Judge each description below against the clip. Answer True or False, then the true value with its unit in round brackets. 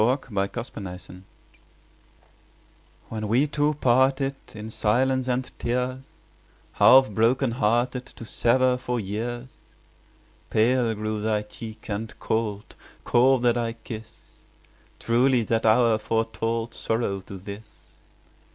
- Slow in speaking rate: True (115 wpm)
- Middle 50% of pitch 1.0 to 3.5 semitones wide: True (2.7 semitones)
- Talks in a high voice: False (115 Hz)